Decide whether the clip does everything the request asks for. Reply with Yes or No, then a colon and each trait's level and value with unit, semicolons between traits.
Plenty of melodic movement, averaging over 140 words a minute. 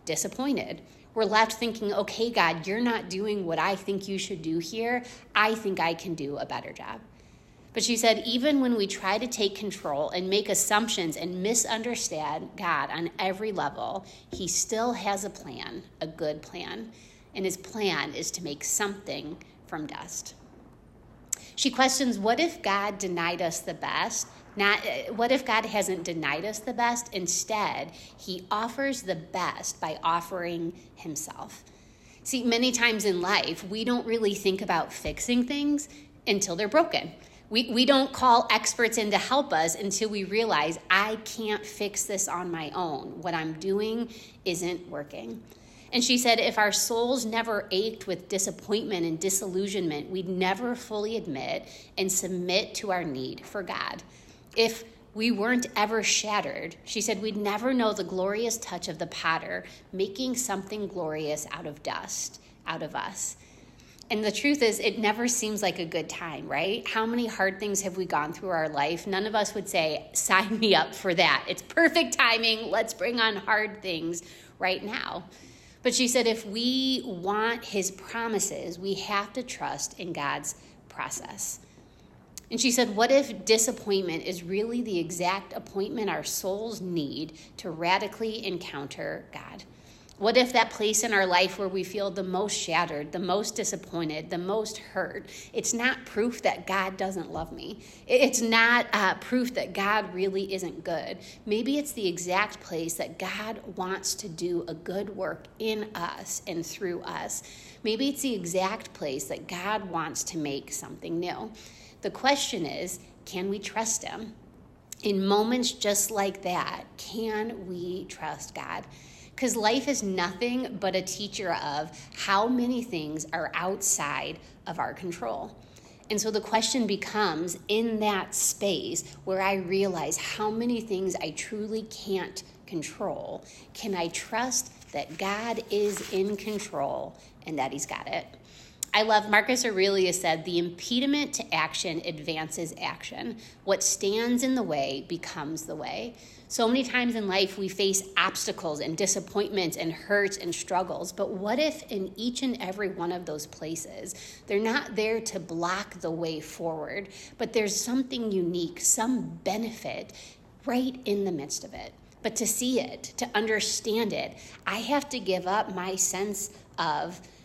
No: average, 3.8 semitones; average, 165 wpm